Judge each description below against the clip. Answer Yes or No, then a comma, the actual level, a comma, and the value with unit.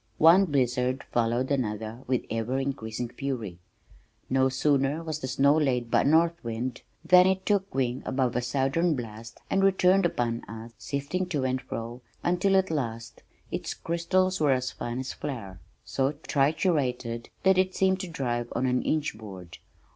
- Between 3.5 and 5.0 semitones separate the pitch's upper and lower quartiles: No, wide, 5.5 semitones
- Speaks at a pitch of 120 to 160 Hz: Yes, low, 135 Hz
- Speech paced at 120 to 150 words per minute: No, average, 165 wpm